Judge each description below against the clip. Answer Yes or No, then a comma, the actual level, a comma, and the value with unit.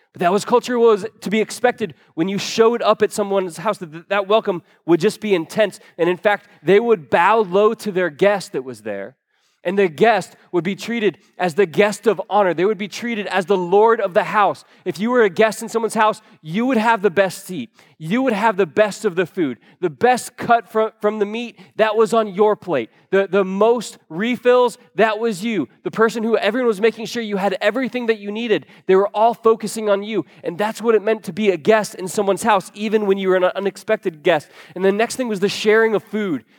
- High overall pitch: Yes, high, 210 Hz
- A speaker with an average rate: No, fast, 235 wpm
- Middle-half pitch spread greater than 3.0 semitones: No, narrow, 2.5 semitones